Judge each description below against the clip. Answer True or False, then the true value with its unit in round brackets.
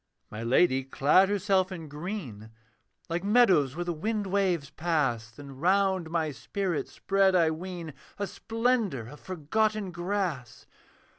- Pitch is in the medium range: True (175 Hz)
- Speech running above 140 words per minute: False (135 wpm)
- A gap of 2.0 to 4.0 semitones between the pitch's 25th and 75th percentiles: False (5.1 semitones)